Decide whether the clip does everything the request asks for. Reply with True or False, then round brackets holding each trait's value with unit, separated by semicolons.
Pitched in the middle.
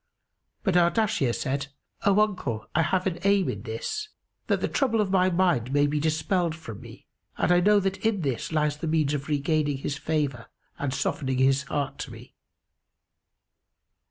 True (155 Hz)